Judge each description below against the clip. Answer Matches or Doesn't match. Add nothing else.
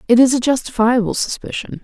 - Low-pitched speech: Doesn't match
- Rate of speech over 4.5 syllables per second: Matches